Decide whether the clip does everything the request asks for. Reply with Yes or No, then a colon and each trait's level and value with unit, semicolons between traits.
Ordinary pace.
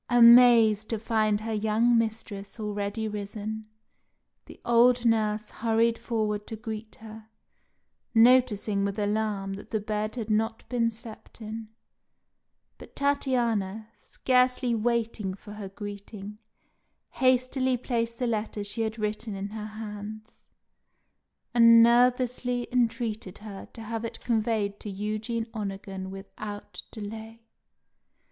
No: slow, 120 wpm